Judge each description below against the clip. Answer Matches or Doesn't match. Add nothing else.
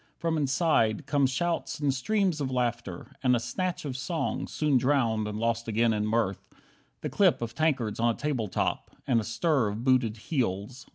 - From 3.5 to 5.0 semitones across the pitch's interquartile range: Matches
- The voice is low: Matches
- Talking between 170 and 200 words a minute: Matches